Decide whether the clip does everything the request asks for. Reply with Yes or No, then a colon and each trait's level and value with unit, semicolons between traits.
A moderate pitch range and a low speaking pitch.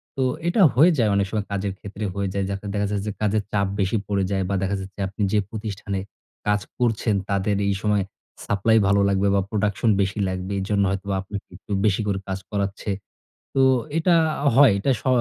No: narrow, 1.5 semitones; low, 100 Hz